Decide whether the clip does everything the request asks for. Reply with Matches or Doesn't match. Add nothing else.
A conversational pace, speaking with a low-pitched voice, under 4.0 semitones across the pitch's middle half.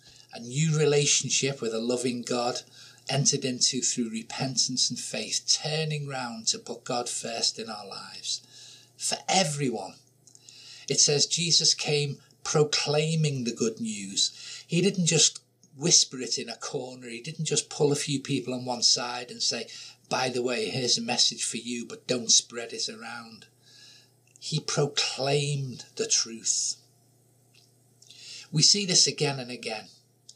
Matches